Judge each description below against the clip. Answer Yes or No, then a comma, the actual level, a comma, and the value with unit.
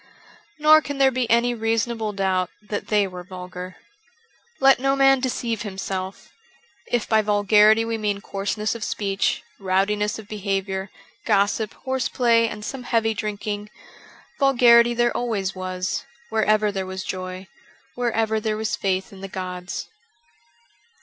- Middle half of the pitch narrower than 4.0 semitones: Yes, average, 3.4 semitones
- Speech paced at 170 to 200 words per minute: No, average, 140 wpm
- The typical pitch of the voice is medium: No, high, 210 Hz